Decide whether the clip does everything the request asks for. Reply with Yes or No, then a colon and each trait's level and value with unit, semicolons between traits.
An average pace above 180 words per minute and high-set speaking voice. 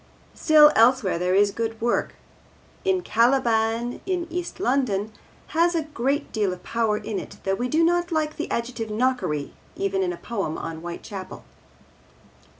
No: average, 155 wpm; high, 235 Hz